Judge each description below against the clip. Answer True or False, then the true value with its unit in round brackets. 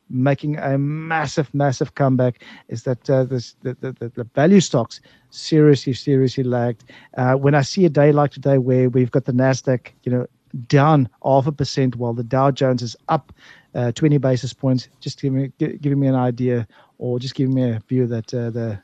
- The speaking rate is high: False (195 wpm)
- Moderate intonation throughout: False (2.1 semitones)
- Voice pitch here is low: True (130 Hz)